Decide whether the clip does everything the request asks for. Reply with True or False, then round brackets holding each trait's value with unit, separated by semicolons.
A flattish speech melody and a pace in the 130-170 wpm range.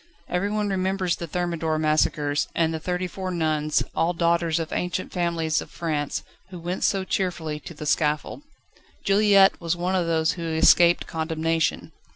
True (2.3 semitones; 160 wpm)